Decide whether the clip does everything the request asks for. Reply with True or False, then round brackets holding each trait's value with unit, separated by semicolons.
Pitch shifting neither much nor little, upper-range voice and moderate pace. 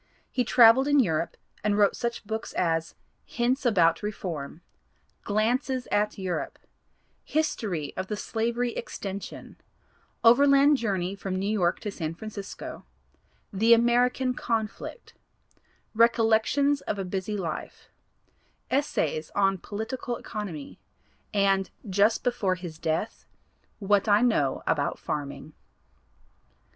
False (4.2 semitones; 210 Hz; 110 wpm)